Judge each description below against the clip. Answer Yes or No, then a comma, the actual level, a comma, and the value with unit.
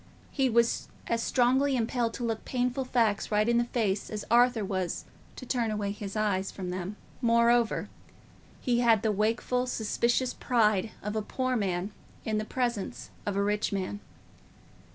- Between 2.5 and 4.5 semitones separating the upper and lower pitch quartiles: Yes, average, 2.8 semitones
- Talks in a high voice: Yes, high, 225 Hz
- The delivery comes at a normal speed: Yes, average, 165 wpm